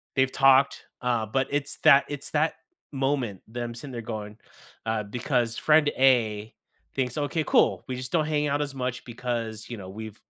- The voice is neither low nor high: No, low, 125 Hz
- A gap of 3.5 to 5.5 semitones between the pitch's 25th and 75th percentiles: Yes, average, 3.8 semitones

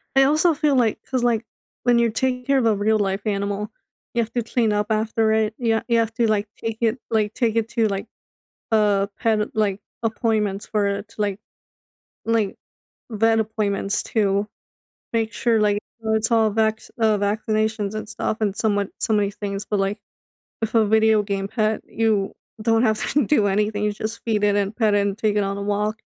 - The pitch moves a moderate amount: No, narrow, 1.6 semitones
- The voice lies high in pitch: Yes, high, 215 Hz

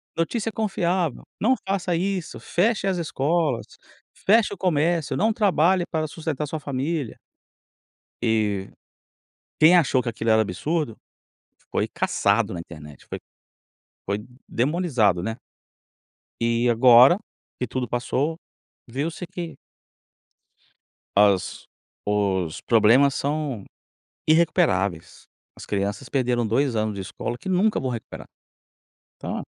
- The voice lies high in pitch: No, low, 135 Hz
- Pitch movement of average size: No, wide, 7.4 semitones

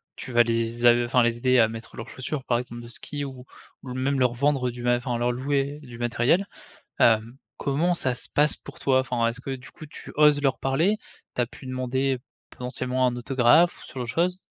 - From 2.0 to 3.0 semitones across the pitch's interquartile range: Yes, narrow, 2.4 semitones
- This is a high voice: No, low, 125 Hz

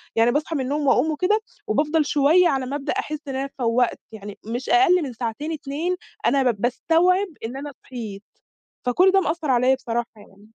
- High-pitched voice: Yes, very high, 275 Hz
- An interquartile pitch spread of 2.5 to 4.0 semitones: No, average, 4.9 semitones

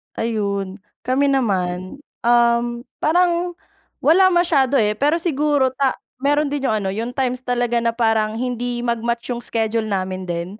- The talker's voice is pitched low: No, high, 240 Hz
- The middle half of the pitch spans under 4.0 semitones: No, average, 4.4 semitones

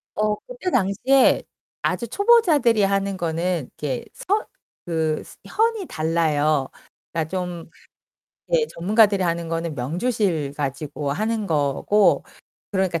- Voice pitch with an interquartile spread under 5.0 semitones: No, wide, 5.6 semitones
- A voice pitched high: No, medium, 180 Hz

